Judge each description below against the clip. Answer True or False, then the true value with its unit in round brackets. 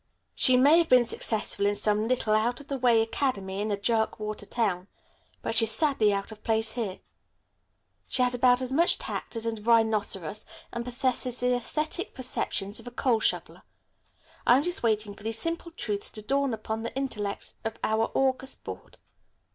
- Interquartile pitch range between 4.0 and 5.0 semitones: False (3.2 semitones)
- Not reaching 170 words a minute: False (180 wpm)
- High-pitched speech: True (230 Hz)